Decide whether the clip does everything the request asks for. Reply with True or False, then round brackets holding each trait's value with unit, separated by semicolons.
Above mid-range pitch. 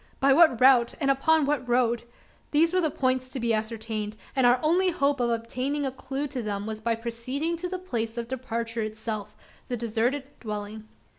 True (245 Hz)